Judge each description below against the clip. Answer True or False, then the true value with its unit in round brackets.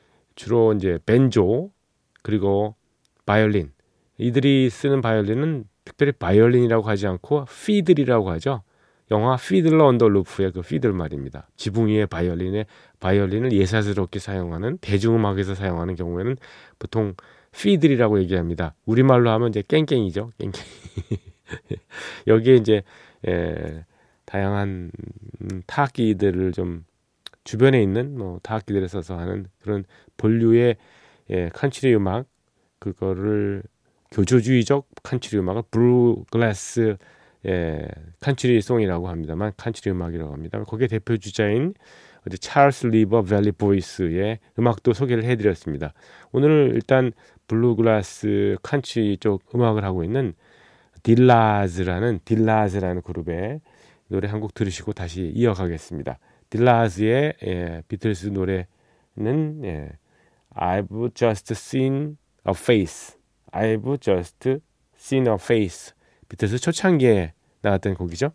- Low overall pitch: True (110 Hz)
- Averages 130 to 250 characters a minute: False (300 characters per minute)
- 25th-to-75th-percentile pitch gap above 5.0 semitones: False (4.2 semitones)